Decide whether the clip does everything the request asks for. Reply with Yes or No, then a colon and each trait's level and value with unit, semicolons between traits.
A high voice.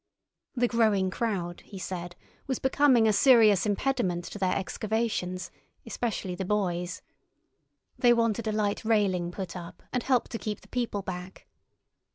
Yes: high, 205 Hz